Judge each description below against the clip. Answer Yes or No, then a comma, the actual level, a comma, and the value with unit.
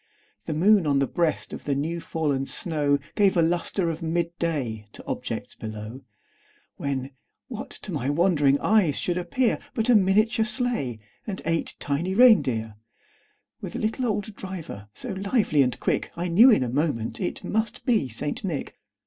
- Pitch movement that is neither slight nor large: No, wide, 6.3 semitones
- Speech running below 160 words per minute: No, average, 175 wpm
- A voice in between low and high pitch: Yes, medium, 170 Hz